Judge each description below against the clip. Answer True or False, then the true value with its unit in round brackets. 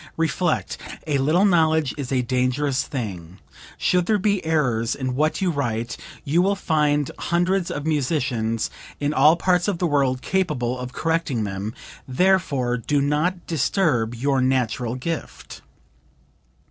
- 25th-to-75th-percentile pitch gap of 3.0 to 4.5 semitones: False (4.9 semitones)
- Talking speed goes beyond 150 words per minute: False (140 wpm)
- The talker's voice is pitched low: False (145 Hz)